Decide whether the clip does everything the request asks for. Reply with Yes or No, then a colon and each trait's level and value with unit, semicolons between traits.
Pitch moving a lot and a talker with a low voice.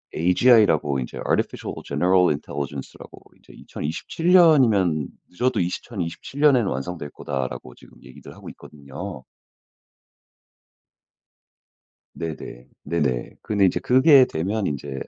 Yes: wide, 8.1 semitones; very low, 90 Hz